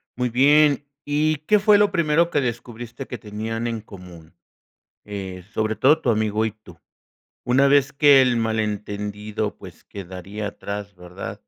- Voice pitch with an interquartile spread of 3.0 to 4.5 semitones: No, average, 5.2 semitones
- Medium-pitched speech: No, low, 110 Hz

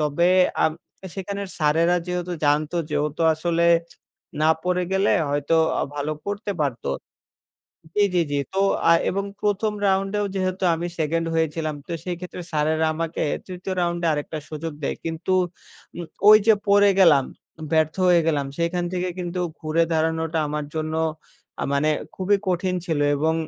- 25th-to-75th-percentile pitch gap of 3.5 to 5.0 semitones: No, average, 3.0 semitones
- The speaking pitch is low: No, medium, 170 Hz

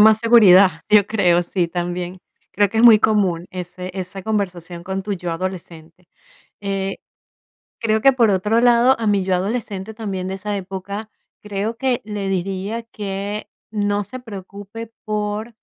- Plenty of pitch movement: No, average, 2.8 semitones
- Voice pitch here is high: Yes, high, 200 Hz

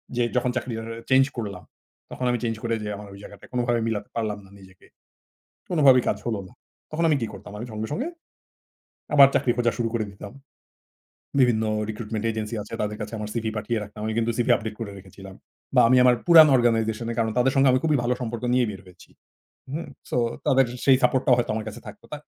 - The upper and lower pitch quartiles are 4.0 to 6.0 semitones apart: No, average, 2.9 semitones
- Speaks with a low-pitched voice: Yes, low, 115 Hz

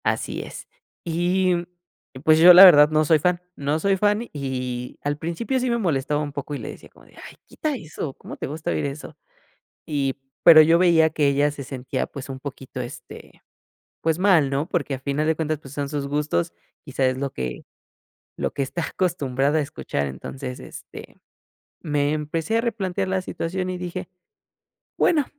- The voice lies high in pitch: No, medium, 155 Hz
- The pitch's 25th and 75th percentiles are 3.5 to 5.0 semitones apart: Yes, average, 4.1 semitones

